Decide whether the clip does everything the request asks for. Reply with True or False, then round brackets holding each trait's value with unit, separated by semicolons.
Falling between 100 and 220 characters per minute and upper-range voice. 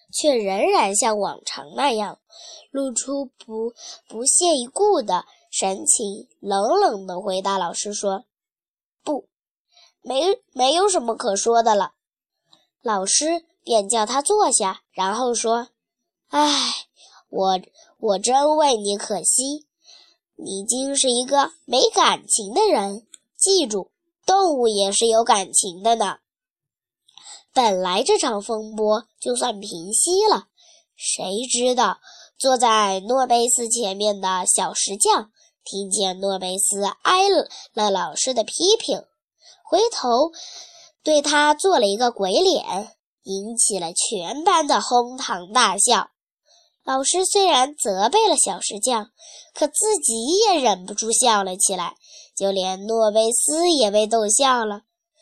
True (175 characters per minute; 245 Hz)